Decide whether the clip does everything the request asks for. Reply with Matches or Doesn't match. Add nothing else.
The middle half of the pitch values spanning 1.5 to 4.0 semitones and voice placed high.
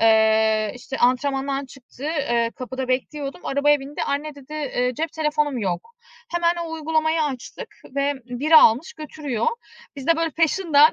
Matches